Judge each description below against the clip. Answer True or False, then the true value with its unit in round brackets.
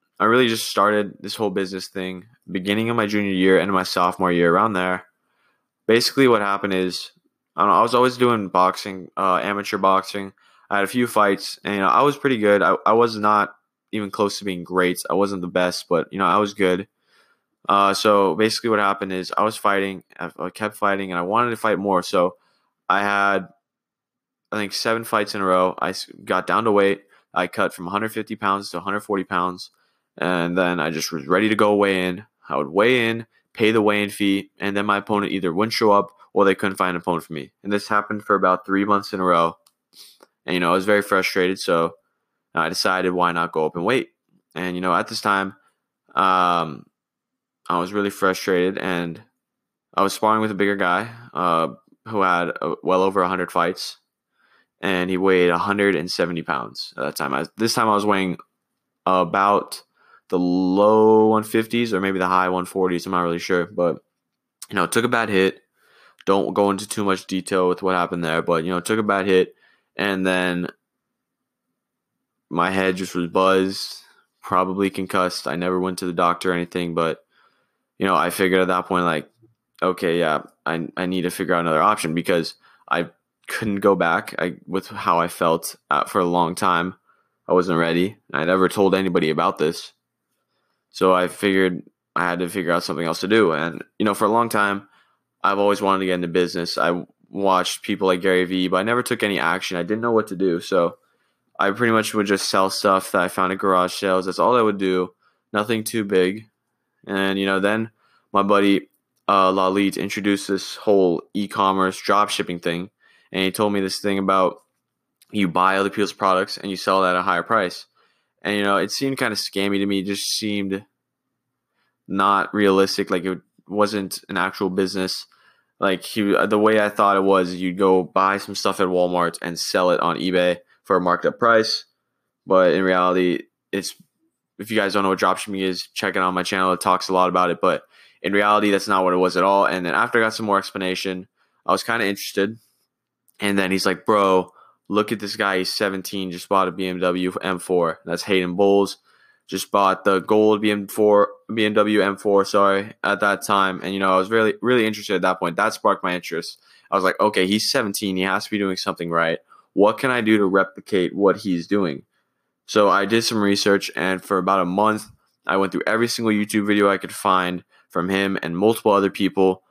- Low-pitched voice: True (95 Hz)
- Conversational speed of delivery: False (210 wpm)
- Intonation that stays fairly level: True (2.1 semitones)